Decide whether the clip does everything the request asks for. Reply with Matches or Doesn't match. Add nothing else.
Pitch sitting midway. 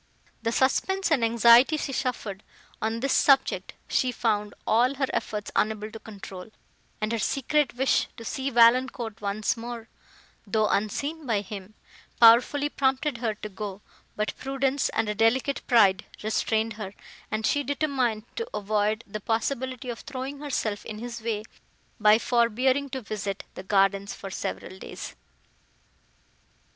Doesn't match